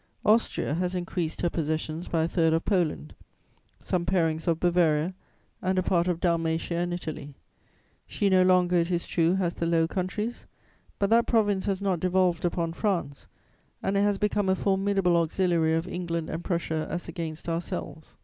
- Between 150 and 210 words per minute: Yes, average, 175 wpm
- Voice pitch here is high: No, medium, 175 Hz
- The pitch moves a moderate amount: No, narrow, 2.3 semitones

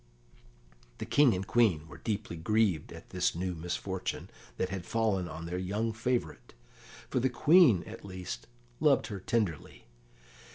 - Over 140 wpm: Yes, average, 150 wpm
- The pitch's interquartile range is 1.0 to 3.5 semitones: No, average, 4.5 semitones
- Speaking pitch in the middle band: No, very low, 95 Hz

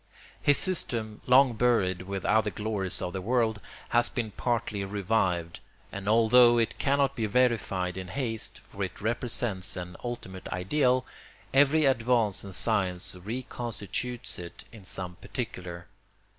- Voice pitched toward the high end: No, low, 110 Hz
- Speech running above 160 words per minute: No, slow, 135 wpm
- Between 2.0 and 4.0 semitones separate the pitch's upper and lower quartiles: No, average, 4.4 semitones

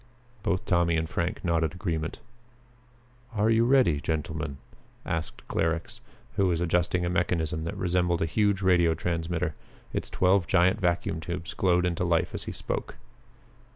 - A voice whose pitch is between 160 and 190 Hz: No, very low, 85 Hz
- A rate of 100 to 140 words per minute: No, average, 150 wpm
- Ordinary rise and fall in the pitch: No, narrow, 1.9 semitones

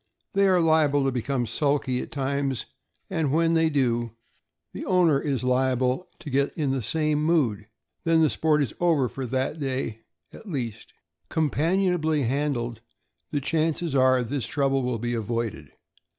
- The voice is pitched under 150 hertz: Yes, medium, 140 Hz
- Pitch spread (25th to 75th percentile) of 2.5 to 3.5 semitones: No, average, 3.9 semitones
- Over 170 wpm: No, average, 155 wpm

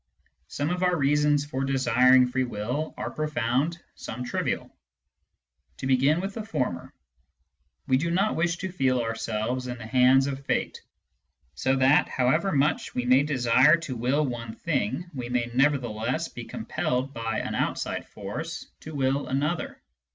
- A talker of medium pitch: No, low, 130 Hz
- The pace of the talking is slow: No, average, 160 wpm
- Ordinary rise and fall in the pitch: Yes, average, 3.2 semitones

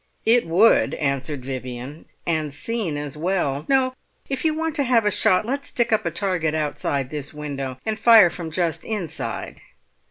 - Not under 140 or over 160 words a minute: No, average, 170 wpm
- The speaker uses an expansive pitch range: Yes, wide, 7.6 semitones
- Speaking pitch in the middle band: Yes, medium, 170 Hz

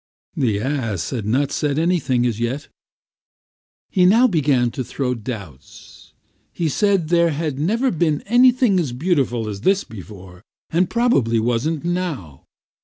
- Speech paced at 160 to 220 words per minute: No, average, 140 wpm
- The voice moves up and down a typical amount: No, wide, 7.3 semitones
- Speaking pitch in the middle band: Yes, medium, 145 Hz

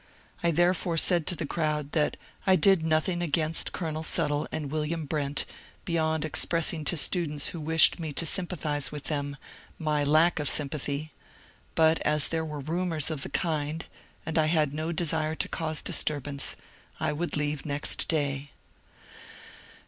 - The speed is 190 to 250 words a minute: No, average, 155 wpm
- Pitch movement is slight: Yes, narrow, 1.9 semitones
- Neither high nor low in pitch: Yes, medium, 155 Hz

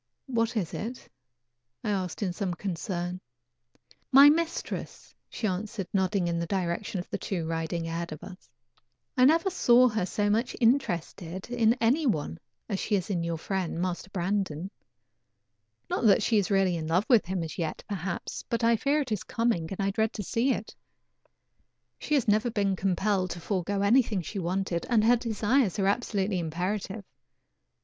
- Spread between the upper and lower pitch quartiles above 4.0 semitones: Yes, average, 4.4 semitones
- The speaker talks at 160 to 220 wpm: Yes, average, 175 wpm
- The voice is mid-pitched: No, high, 195 Hz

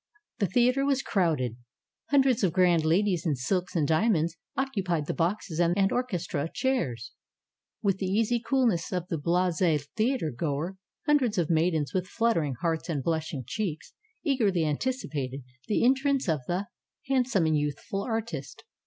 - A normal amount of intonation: No, wide, 6.3 semitones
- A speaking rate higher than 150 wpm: No, average, 145 wpm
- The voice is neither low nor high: Yes, medium, 180 Hz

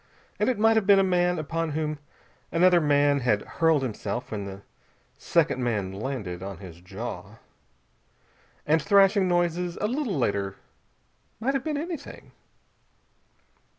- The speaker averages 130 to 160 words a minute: Yes, average, 140 wpm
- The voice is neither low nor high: Yes, medium, 155 Hz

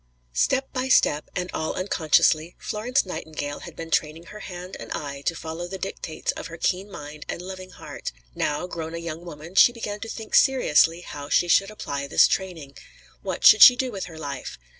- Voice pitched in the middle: Yes, medium, 170 Hz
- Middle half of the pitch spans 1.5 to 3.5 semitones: No, average, 4.0 semitones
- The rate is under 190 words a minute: No, average, 200 wpm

